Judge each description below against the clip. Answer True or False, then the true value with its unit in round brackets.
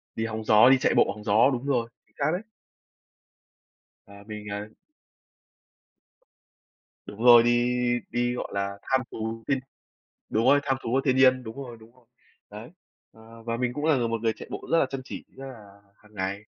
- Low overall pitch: True (115 Hz)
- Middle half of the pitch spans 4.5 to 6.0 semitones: False (3.0 semitones)